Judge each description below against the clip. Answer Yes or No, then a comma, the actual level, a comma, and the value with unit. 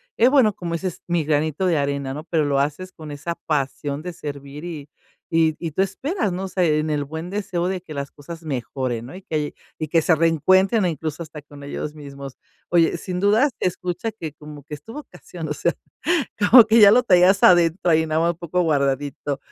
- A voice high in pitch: No, medium, 160 Hz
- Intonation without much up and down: No, average, 3.7 semitones